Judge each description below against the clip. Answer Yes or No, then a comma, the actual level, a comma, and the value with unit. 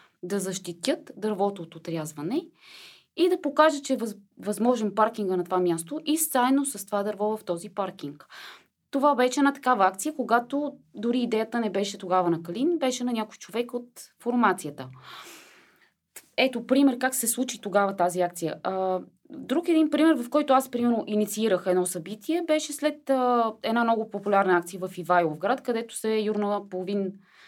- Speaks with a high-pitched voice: Yes, high, 220 Hz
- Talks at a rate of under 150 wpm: No, average, 160 wpm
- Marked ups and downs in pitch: Yes, wide, 5.8 semitones